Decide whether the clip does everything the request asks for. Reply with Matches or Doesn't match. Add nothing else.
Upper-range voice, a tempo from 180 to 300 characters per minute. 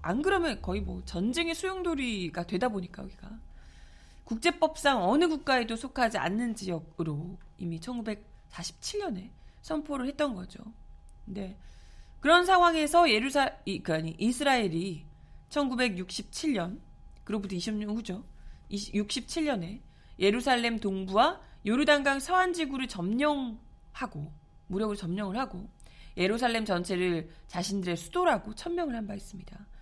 Matches